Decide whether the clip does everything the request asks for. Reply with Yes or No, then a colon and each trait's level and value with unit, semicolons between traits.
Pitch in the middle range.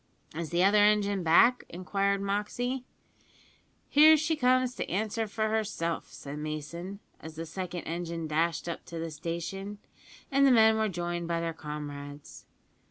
Yes: medium, 180 Hz